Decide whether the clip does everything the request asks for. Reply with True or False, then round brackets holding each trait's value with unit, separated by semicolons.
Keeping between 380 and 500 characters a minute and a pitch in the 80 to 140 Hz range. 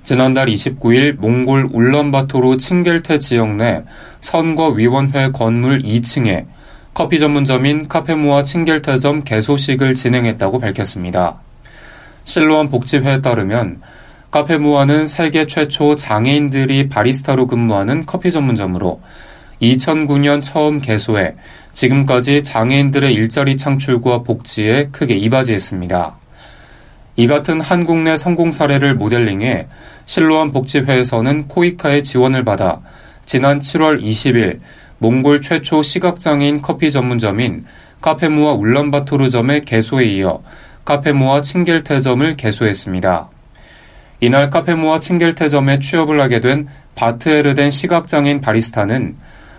False (295 characters per minute; 135 Hz)